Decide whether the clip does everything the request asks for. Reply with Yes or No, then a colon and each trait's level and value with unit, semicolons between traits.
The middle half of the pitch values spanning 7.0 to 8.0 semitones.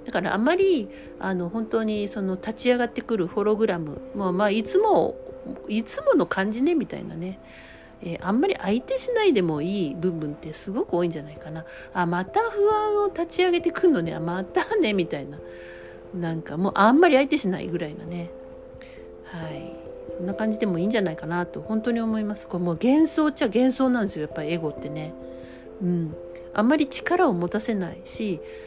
Yes: wide, 7.4 semitones